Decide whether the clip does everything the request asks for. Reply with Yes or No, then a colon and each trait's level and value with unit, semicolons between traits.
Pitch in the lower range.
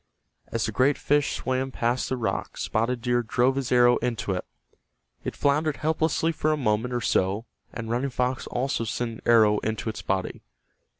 Yes: low, 120 Hz